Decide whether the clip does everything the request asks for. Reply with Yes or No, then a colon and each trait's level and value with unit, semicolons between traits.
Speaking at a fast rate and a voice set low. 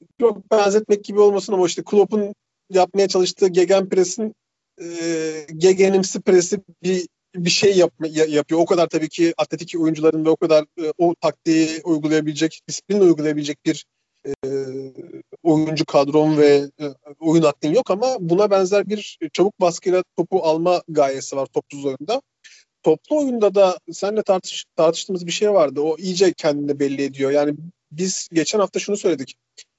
No: fast, 150 wpm; medium, 170 Hz